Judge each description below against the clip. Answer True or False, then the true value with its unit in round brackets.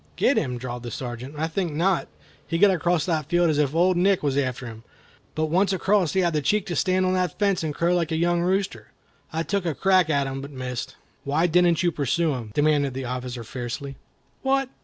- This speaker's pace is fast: True (225 wpm)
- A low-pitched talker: False (160 Hz)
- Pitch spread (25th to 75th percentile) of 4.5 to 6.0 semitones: True (5.0 semitones)